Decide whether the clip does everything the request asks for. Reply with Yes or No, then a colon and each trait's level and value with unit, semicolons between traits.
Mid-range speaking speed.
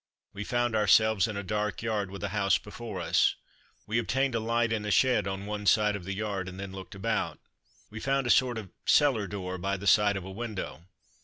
No: fast, 225 wpm